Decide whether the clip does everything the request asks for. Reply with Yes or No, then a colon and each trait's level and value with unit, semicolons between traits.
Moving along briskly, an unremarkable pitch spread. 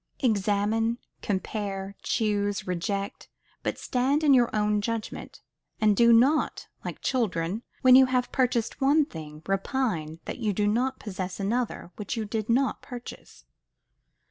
No: average, 140 wpm; average, 3.9 semitones